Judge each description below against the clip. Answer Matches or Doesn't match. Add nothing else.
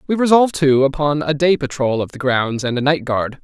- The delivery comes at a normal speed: Doesn't match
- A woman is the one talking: Doesn't match